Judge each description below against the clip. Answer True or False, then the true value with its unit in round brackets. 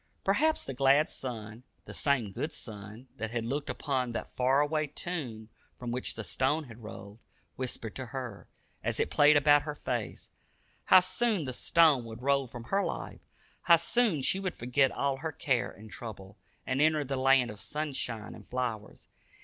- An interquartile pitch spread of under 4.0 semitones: False (4.4 semitones)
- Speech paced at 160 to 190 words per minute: True (180 wpm)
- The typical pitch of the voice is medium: False (130 Hz)